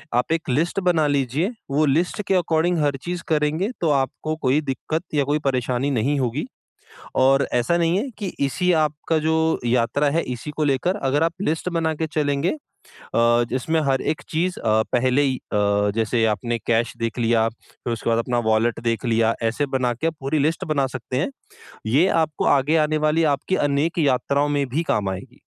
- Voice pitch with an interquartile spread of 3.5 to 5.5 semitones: Yes, average, 4.7 semitones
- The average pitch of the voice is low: No, medium, 145 Hz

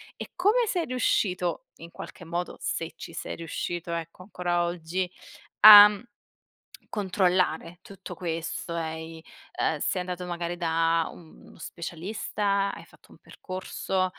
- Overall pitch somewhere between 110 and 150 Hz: No, medium, 175 Hz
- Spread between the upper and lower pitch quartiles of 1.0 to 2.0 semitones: No, narrow, 2.5 semitones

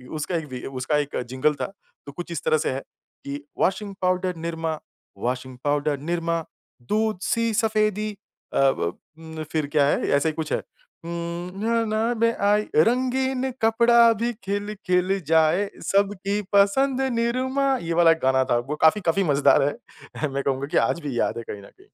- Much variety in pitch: Yes, wide, 6.3 semitones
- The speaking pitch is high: No, medium, 175 Hz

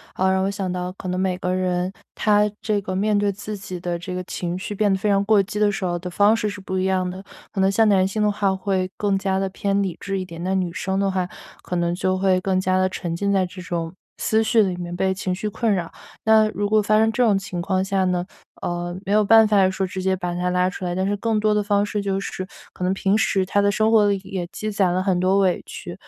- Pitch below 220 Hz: Yes, high, 190 Hz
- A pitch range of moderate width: No, narrow, 1.9 semitones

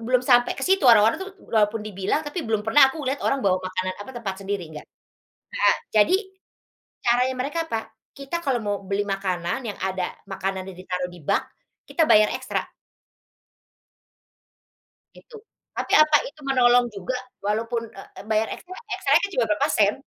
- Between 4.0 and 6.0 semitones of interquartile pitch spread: Yes, average, 5.2 semitones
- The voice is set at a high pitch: Yes, high, 220 Hz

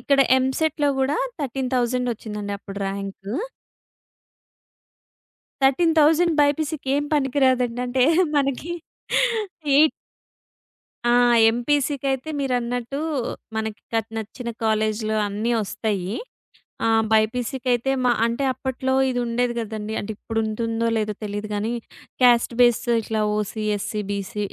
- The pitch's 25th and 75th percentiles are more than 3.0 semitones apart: Yes, average, 3.7 semitones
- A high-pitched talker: Yes, high, 240 Hz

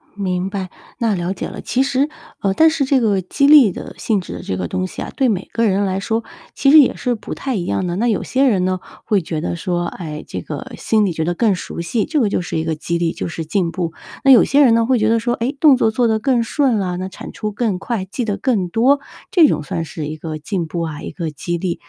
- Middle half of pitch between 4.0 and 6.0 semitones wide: Yes, wide, 5.6 semitones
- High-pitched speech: Yes, high, 200 Hz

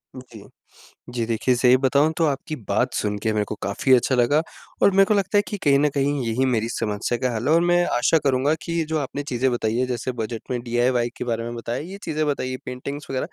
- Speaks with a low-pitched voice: Yes, low, 130 Hz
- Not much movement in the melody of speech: No, average, 3.6 semitones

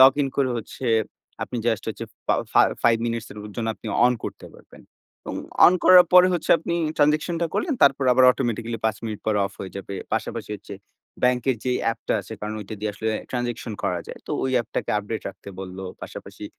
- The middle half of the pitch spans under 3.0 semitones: No, average, 3.7 semitones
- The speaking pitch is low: Yes, low, 115 Hz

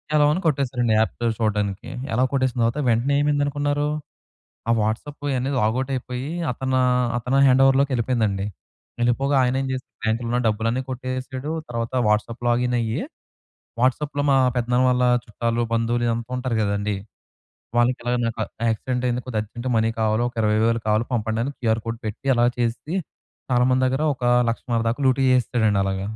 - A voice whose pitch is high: No, low, 120 Hz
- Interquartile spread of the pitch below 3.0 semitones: Yes, narrow, 2.5 semitones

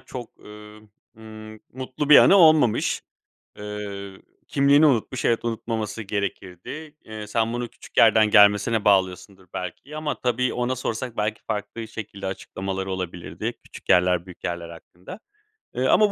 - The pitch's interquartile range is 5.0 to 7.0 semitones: No, average, 3.9 semitones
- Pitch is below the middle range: Yes, low, 110 Hz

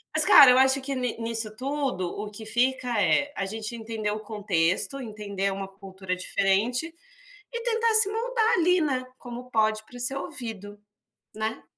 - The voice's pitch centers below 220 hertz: No, high, 230 Hz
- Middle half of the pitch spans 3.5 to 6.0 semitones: Yes, average, 4.5 semitones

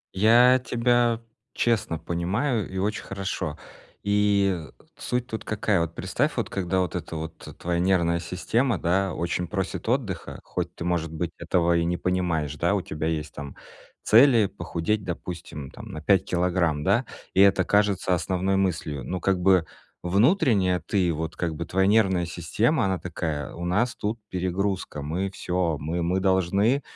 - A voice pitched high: No, very low, 90 Hz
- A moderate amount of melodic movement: Yes, average, 3.3 semitones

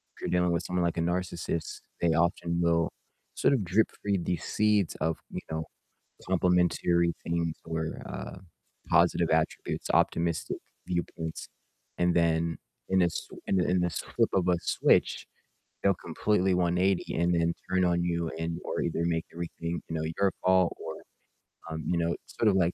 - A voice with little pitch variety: Yes, narrow, 1.4 semitones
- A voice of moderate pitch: No, very low, 85 Hz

